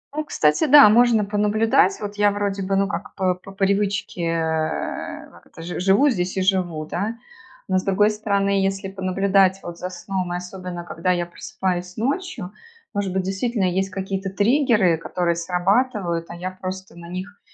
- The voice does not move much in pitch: Yes, narrow, 2.3 semitones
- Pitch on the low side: No, high, 190 Hz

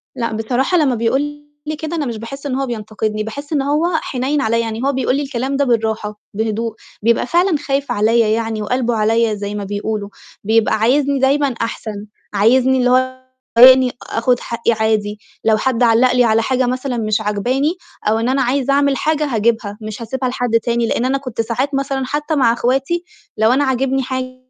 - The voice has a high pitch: Yes, high, 245 Hz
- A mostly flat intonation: No, average, 3.4 semitones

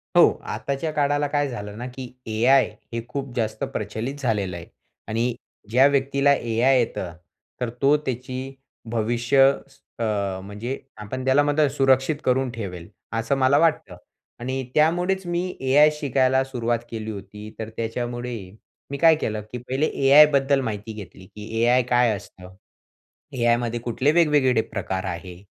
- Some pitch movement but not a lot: Yes, average, 3.6 semitones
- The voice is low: Yes, low, 125 Hz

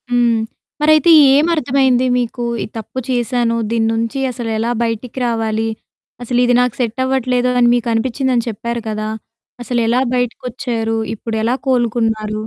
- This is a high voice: Yes, high, 240 Hz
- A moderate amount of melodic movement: No, narrow, 1.9 semitones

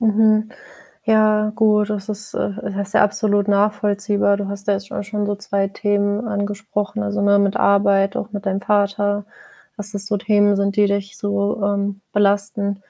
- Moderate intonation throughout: No, narrow, 0.8 semitones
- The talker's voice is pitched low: No, high, 205 Hz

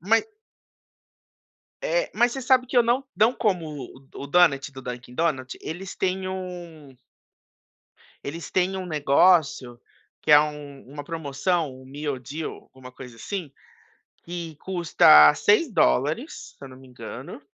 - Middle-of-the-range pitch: Yes, medium, 160 Hz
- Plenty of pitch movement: Yes, wide, 5.7 semitones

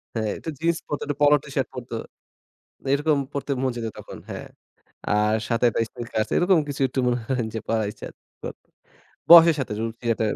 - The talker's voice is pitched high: No, low, 125 Hz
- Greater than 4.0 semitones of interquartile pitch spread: Yes, average, 4.6 semitones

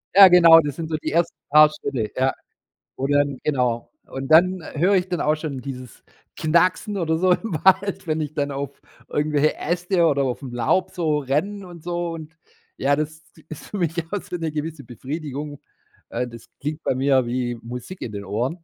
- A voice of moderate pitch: Yes, medium, 155 Hz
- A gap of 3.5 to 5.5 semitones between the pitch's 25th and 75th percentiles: Yes, average, 4.0 semitones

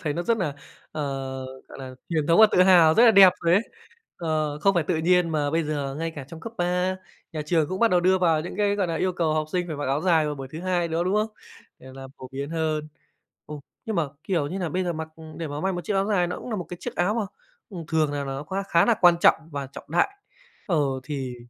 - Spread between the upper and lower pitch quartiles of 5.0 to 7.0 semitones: No, average, 3.4 semitones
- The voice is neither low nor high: Yes, medium, 165 Hz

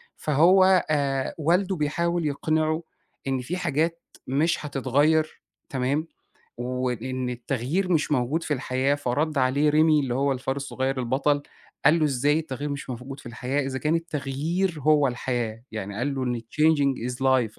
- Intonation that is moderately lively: Yes, average, 3.4 semitones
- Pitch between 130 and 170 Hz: Yes, medium, 140 Hz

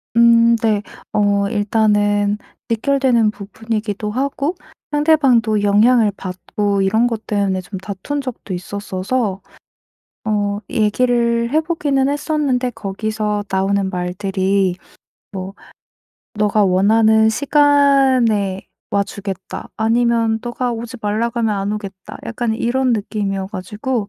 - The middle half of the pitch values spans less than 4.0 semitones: Yes, average, 3.1 semitones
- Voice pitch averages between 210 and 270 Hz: Yes, high, 215 Hz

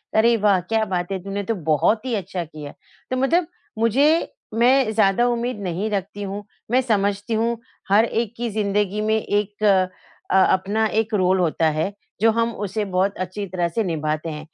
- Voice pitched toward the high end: Yes, high, 205 Hz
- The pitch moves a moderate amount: Yes, average, 3.3 semitones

